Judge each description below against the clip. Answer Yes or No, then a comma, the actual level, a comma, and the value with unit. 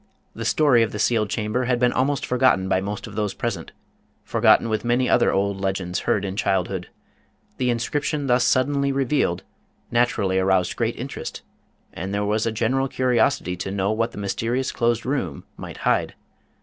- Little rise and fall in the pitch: No, average, 4.4 semitones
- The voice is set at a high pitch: No, low, 115 Hz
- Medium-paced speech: Yes, average, 180 wpm